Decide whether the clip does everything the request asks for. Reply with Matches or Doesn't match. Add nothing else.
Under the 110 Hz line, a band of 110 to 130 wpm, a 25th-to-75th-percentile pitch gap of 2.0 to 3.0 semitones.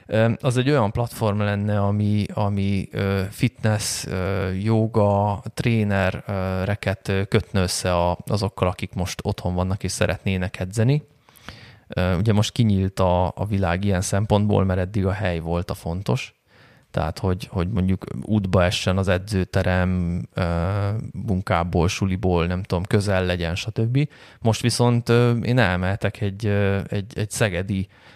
Matches